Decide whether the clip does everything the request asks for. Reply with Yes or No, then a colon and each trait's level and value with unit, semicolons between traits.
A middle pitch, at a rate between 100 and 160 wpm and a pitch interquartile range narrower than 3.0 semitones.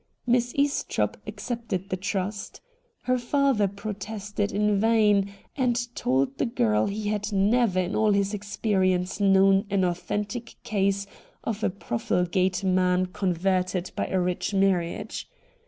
No: high, 200 Hz; slow, 135 wpm; narrow, 2.6 semitones